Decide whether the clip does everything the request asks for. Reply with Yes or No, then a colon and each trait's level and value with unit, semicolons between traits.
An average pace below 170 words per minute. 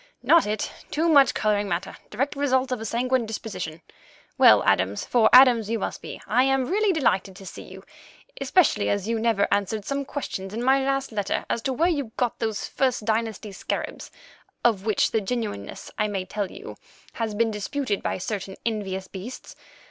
No: average, 180 wpm